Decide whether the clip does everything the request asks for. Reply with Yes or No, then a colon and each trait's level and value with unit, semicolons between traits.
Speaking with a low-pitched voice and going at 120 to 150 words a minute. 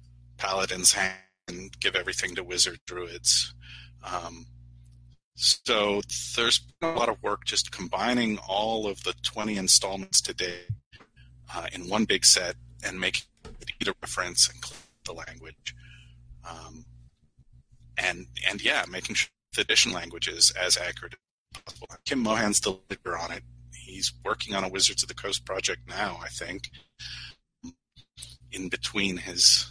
Yes: very low, 85 Hz; average, 140 wpm